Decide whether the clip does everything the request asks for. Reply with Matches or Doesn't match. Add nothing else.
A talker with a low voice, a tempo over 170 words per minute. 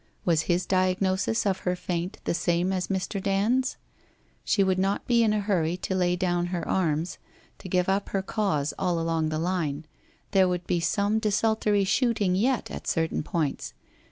Doesn't match